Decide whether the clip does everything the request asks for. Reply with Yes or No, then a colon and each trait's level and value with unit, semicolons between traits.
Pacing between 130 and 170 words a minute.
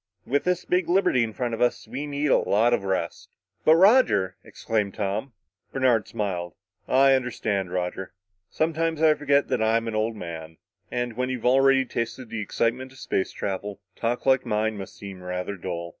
No: average, 180 wpm